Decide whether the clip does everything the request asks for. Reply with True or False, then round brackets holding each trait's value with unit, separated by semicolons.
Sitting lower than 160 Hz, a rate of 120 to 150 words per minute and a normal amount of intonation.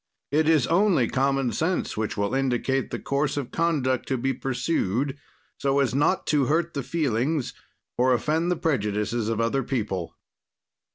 False (135 Hz; 160 wpm; 4.3 semitones)